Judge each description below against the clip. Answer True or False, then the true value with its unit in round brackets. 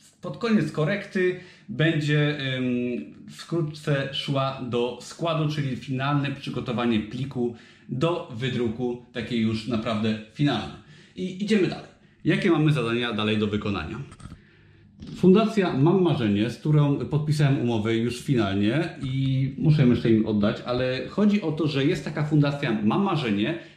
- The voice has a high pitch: False (135 Hz)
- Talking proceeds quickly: False (130 wpm)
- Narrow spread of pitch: False (5.2 semitones)